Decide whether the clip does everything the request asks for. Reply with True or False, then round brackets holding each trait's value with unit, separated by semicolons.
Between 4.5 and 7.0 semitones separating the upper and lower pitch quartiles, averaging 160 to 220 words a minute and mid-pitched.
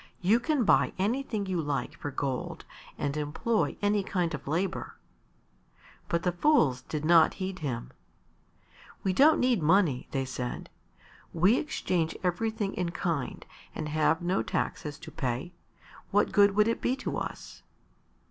False (5.5 semitones; 150 wpm; 180 Hz)